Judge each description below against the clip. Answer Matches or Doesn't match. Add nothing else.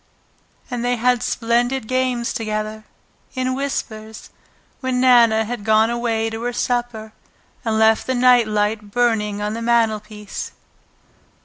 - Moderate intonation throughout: Doesn't match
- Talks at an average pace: Doesn't match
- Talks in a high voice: Matches